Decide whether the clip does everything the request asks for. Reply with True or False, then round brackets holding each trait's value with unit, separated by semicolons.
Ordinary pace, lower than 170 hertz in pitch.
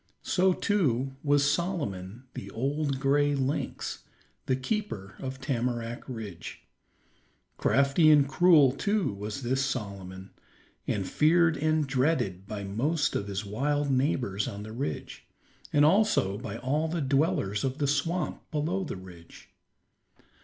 False (130 wpm; 135 Hz)